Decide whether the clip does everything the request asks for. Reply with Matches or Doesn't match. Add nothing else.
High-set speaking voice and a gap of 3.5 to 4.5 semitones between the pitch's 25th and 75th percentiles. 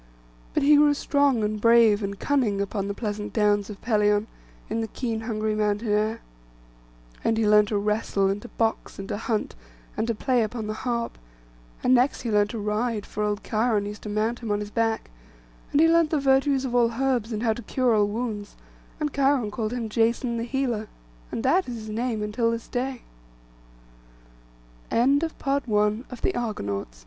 Doesn't match